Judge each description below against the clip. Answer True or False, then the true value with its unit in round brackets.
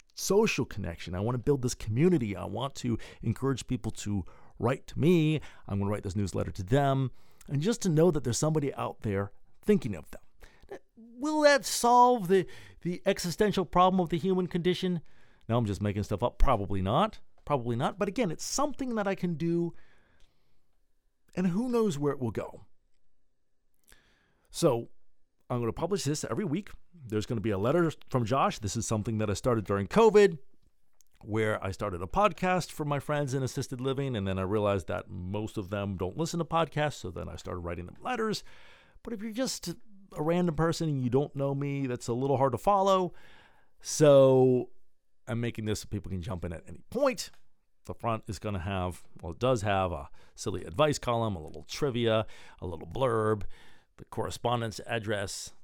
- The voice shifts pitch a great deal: True (8.6 semitones)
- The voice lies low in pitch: True (130 Hz)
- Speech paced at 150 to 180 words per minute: False (195 wpm)